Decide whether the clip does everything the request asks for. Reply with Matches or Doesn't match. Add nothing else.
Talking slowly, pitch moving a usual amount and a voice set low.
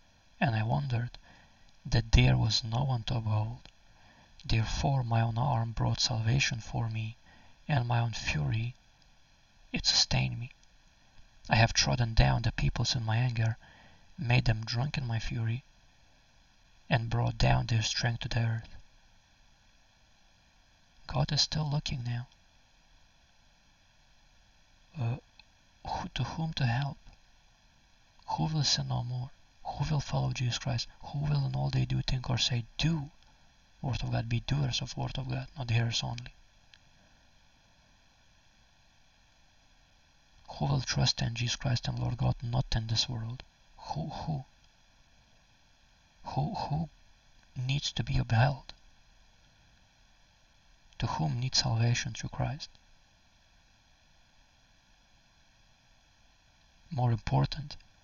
Matches